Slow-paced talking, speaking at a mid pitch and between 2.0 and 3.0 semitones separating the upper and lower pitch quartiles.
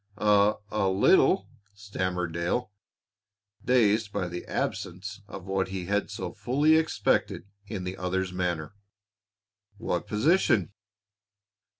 No: slow, 110 wpm; low, 100 Hz; average, 2.7 semitones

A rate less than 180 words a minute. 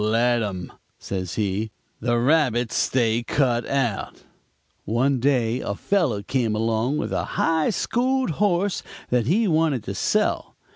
Yes: average, 140 wpm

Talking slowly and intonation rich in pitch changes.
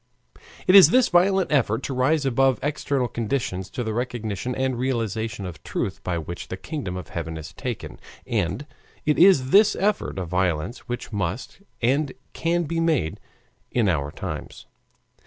No: average, 160 wpm; wide, 8.0 semitones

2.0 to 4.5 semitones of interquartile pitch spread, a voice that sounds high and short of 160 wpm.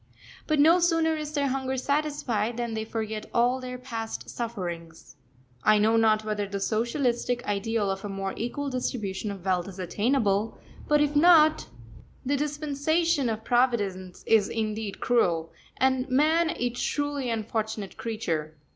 No: average, 5.2 semitones; high, 235 Hz; average, 145 wpm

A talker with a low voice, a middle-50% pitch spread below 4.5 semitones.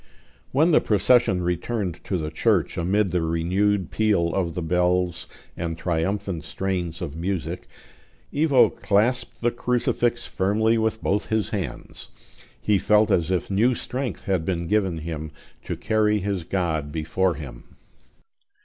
Yes: very low, 95 Hz; average, 4.1 semitones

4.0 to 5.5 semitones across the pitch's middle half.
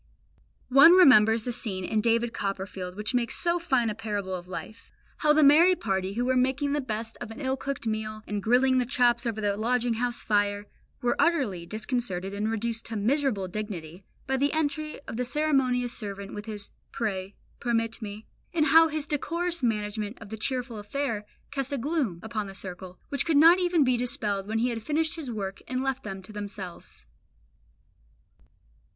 Yes: average, 4.7 semitones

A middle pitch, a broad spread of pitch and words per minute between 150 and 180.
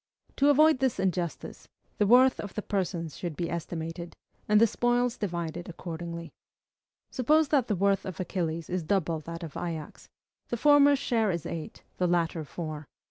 Yes: medium, 180 Hz; wide, 5.7 semitones; average, 165 wpm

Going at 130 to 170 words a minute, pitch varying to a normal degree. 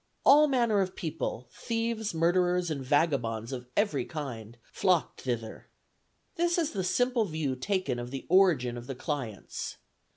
No: average, 150 wpm; wide, 8.2 semitones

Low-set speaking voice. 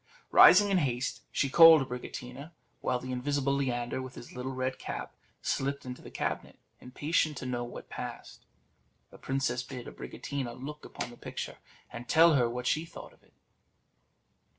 Yes: low, 130 Hz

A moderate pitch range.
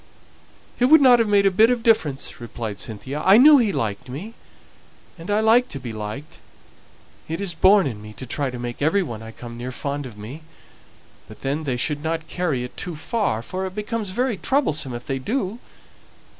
No: wide, 9.0 semitones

